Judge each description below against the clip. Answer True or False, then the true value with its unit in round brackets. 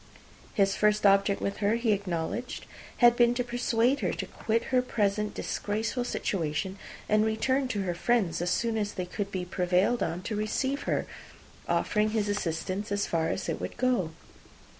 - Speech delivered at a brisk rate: False (175 wpm)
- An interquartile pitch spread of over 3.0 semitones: True (3.7 semitones)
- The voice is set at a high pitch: True (210 Hz)